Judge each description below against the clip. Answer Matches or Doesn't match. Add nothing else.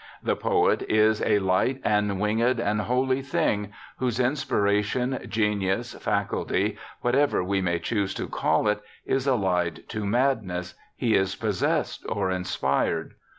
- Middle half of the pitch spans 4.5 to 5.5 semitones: Doesn't match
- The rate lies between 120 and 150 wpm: Matches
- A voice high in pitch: Doesn't match